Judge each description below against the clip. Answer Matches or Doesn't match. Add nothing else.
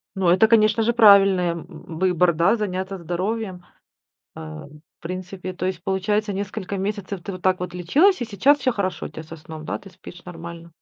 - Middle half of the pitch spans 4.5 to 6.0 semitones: Doesn't match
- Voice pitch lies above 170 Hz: Matches